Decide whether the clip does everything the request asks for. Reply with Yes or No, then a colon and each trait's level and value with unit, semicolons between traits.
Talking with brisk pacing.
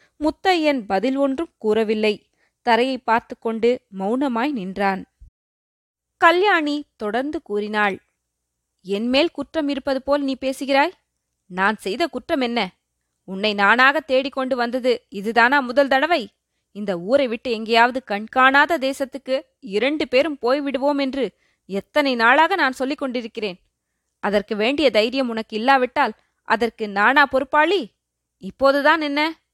No: average, 110 wpm